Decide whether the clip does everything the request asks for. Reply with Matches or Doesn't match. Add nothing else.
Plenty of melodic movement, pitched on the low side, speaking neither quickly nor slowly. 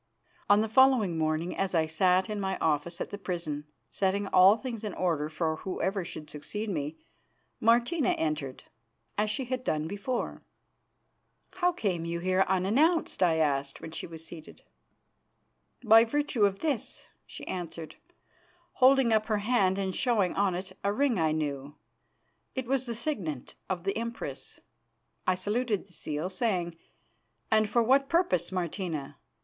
Doesn't match